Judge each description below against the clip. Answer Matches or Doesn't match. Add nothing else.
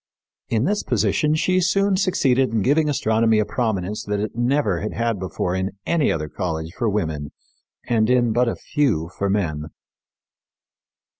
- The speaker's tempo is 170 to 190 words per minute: Doesn't match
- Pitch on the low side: Matches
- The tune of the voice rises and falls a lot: Matches